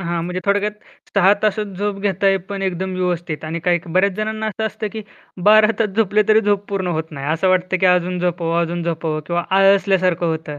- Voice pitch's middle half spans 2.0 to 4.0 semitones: Yes, average, 2.9 semitones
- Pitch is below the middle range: No, medium, 185 Hz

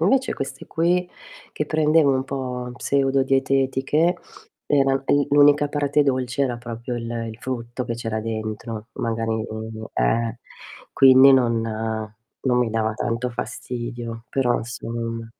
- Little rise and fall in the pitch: No, average, 3.0 semitones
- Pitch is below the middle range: Yes, low, 125 Hz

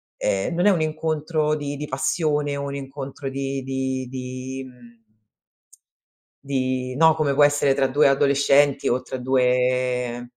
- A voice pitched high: No, low, 135 Hz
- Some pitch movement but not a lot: No, narrow, 2.2 semitones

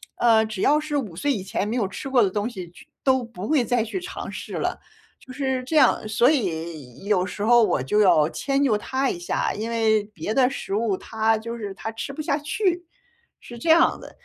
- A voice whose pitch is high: Yes, high, 225 Hz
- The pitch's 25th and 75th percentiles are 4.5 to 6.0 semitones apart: Yes, average, 4.8 semitones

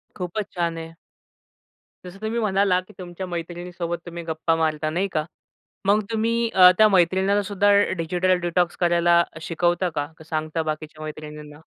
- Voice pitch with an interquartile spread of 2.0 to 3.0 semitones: Yes, narrow, 2.6 semitones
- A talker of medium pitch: Yes, medium, 175 Hz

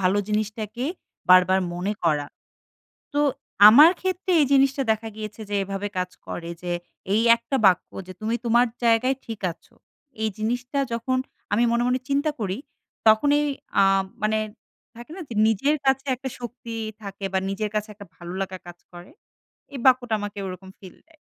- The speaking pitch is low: No, high, 220 Hz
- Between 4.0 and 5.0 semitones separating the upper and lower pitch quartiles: Yes, average, 4.7 semitones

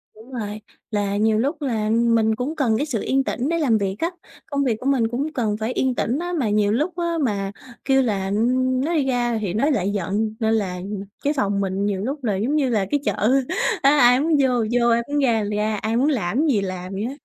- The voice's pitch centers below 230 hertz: No, high, 235 Hz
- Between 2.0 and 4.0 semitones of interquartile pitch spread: No, average, 4.5 semitones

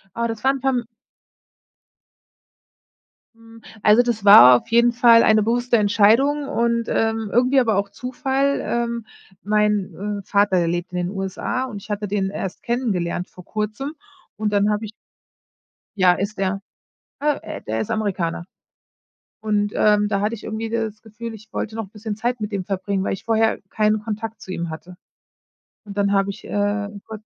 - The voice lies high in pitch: Yes, high, 215 Hz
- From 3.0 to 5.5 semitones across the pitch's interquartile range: No, narrow, 2.5 semitones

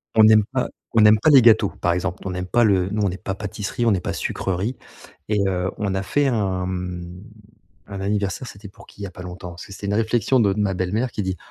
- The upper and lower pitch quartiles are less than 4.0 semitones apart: Yes, average, 2.7 semitones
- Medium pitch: No, low, 100 Hz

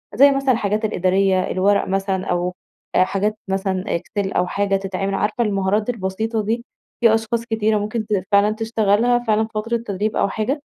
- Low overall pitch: No, high, 210 Hz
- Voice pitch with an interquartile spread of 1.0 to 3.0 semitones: Yes, narrow, 2.5 semitones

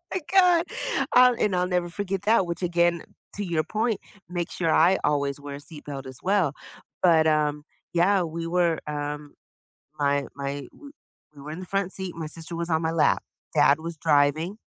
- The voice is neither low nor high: Yes, medium, 170 Hz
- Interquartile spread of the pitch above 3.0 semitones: Yes, average, 3.9 semitones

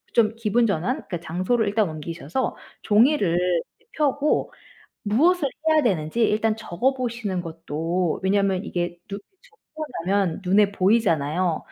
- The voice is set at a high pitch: Yes, high, 200 Hz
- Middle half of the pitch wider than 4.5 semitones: Yes, average, 5.1 semitones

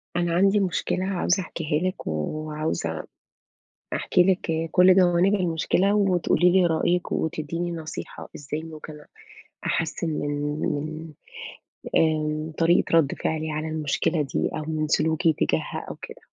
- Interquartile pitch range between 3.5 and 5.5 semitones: No, narrow, 2.4 semitones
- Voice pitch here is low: No, medium, 160 Hz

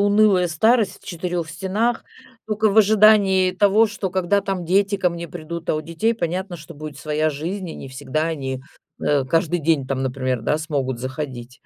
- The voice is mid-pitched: Yes, medium, 170 Hz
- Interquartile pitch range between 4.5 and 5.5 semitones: Yes, average, 5.0 semitones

